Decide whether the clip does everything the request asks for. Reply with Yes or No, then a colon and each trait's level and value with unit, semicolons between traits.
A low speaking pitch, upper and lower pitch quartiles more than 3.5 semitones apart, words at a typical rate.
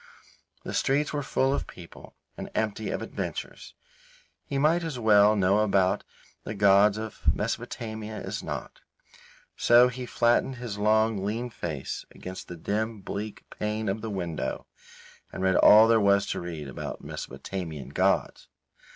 No: low, 105 Hz; average, 2.9 semitones; average, 150 wpm